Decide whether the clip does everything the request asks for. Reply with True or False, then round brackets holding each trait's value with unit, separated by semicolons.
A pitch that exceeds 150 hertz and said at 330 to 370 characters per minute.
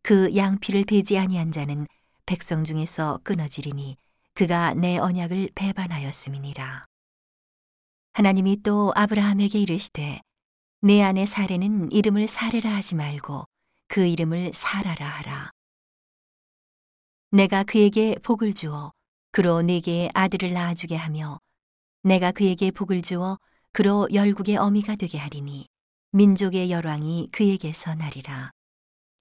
False (185 Hz; 270 characters per minute)